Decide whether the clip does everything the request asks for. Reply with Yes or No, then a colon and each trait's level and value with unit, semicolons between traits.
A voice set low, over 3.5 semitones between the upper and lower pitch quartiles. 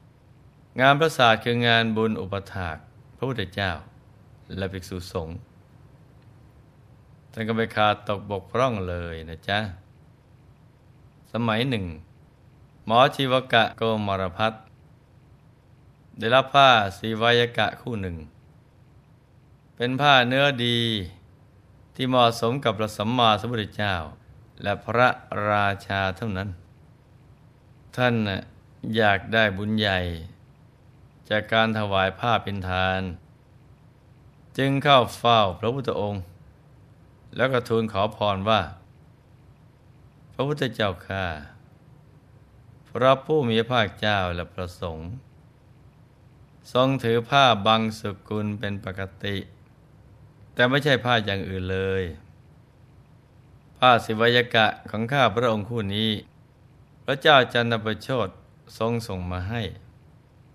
Yes: low, 115 Hz; average, 4.2 semitones